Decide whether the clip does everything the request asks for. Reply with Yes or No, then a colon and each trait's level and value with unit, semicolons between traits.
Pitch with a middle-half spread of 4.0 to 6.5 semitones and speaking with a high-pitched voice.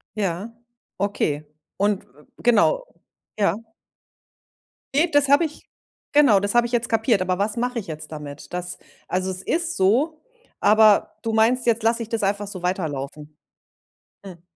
Yes: average, 4.7 semitones; high, 205 Hz